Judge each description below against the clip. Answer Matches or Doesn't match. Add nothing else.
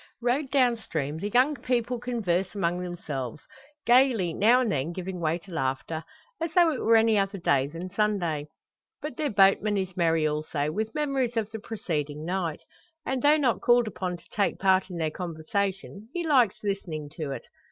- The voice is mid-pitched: Doesn't match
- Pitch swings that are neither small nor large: Doesn't match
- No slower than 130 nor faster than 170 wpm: Doesn't match